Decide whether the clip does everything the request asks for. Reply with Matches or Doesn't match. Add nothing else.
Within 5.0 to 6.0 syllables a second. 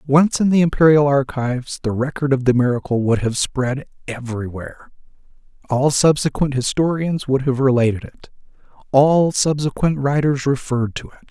Matches